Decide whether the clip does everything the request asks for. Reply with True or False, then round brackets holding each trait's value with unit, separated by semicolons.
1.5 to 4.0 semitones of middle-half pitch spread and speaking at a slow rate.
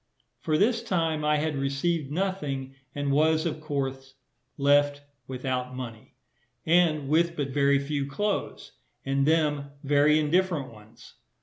True (2.6 semitones; 130 wpm)